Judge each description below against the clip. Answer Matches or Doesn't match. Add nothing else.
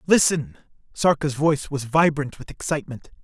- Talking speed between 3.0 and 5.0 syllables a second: Doesn't match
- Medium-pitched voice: Matches